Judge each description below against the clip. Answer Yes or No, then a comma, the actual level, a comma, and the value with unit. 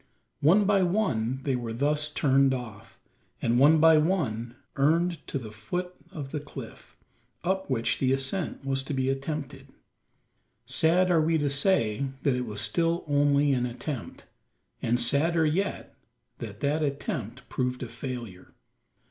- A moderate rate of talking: Yes, average, 150 wpm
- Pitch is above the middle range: No, medium, 140 Hz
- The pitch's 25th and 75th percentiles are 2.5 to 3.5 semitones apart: No, average, 4.3 semitones